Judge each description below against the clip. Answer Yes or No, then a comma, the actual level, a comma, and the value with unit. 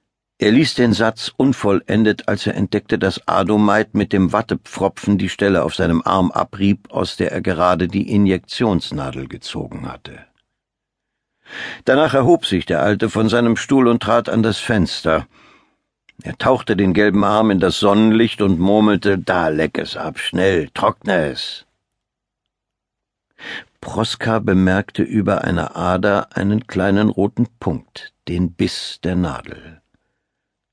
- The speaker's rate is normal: Yes, average, 135 wpm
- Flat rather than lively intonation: No, average, 3.0 semitones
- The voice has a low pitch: Yes, low, 105 Hz